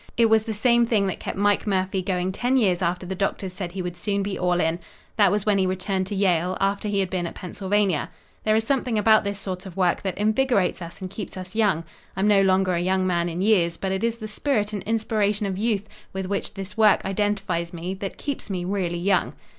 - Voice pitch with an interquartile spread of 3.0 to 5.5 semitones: No, narrow, 2.4 semitones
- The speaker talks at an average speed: No, fast, 240 wpm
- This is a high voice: Yes, high, 195 Hz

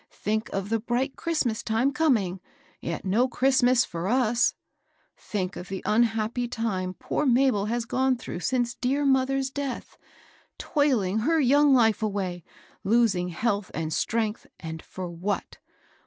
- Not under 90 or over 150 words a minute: Yes, average, 145 wpm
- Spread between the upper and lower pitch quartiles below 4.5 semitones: No, average, 4.9 semitones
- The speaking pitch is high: Yes, high, 230 Hz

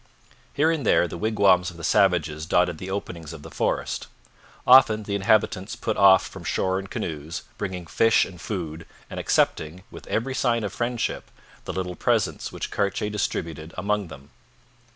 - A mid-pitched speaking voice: No, very low, 95 Hz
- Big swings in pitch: No, average, 4.0 semitones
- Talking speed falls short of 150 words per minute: No, average, 170 wpm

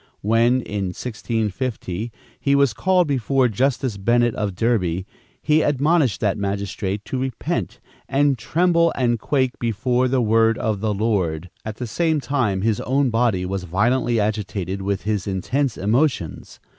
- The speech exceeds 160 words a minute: No, average, 145 wpm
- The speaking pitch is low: Yes, low, 115 Hz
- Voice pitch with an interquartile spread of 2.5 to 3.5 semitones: No, average, 4.5 semitones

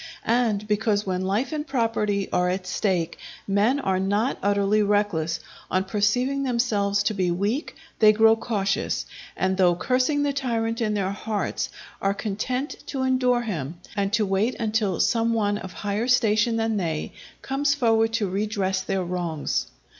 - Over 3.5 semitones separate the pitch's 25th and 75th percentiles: No, average, 3.2 semitones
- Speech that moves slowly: No, average, 160 wpm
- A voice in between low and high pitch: No, high, 210 Hz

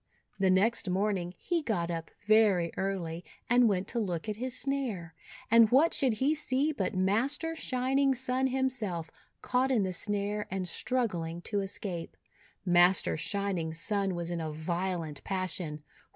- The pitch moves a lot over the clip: Yes, wide, 6.2 semitones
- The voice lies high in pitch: Yes, high, 200 Hz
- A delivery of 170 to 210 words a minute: No, average, 150 wpm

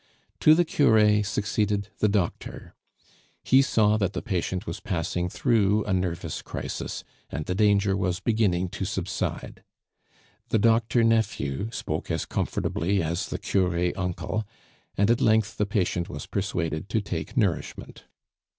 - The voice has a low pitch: Yes, low, 100 Hz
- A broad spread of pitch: No, average, 3.3 semitones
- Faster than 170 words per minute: No, average, 140 wpm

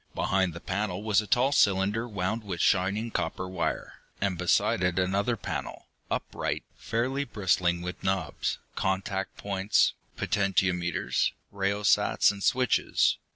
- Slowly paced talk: Yes, slow, 125 wpm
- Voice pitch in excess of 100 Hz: No, very low, 95 Hz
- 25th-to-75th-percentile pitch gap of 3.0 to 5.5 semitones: No, narrow, 2.5 semitones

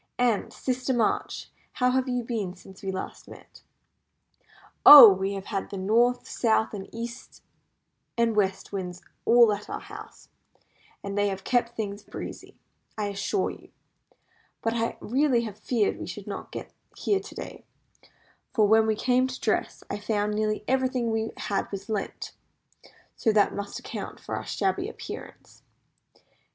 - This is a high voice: Yes, high, 220 Hz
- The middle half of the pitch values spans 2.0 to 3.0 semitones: No, average, 3.4 semitones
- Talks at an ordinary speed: Yes, average, 155 wpm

